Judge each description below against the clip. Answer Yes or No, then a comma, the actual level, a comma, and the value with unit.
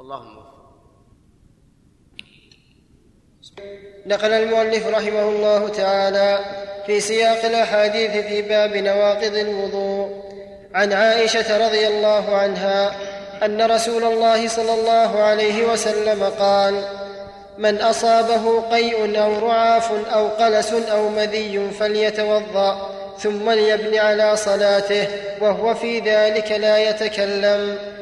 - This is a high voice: Yes, high, 210 Hz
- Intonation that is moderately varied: No, narrow, 1.6 semitones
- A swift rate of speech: No, average, 95 wpm